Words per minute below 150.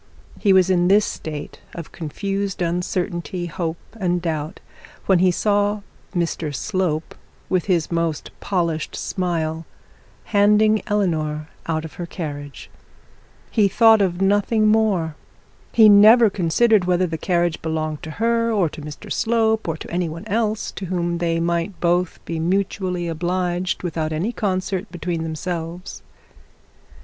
Yes: average, 140 wpm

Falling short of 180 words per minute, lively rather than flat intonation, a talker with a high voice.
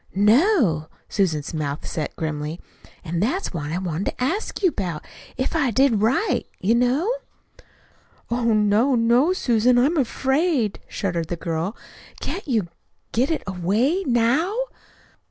Yes: slow, 135 wpm; wide, 7.5 semitones; high, 230 Hz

